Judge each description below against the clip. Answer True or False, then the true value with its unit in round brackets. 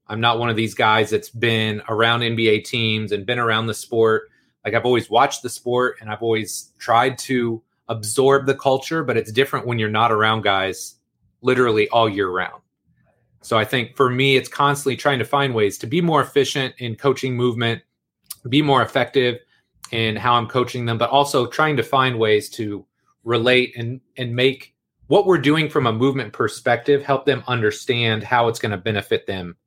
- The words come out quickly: False (190 wpm)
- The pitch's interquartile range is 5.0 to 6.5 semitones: False (3.3 semitones)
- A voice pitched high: False (120 Hz)